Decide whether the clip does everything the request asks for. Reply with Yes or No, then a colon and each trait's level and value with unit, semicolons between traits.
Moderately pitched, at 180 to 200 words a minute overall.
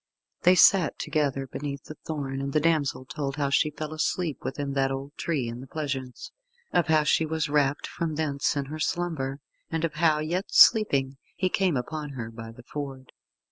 Yes: medium, 145 Hz; average, 195 wpm